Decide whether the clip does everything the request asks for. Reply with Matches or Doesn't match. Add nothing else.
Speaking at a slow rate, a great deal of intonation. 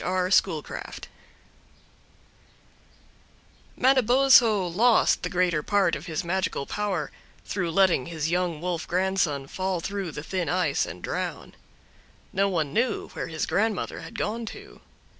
Doesn't match